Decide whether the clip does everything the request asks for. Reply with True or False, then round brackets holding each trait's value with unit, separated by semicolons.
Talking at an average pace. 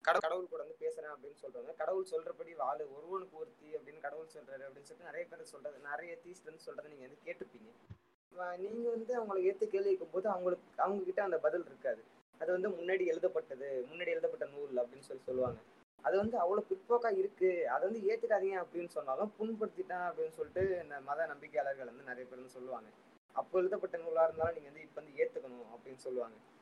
False (180 wpm)